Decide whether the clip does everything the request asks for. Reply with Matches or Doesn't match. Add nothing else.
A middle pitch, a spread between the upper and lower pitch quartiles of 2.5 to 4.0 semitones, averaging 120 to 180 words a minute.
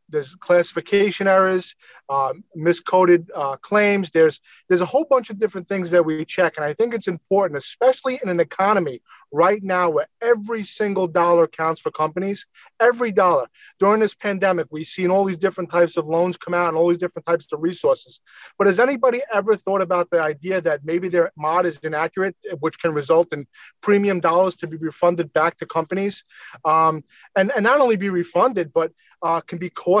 Doesn't match